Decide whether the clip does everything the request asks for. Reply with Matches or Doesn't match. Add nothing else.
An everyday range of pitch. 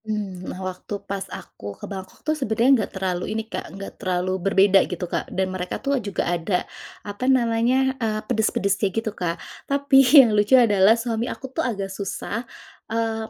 Matches